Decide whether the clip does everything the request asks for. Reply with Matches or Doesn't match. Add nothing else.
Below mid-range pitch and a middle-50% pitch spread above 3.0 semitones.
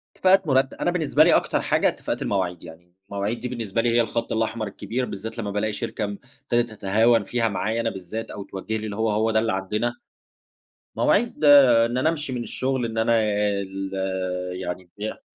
Matches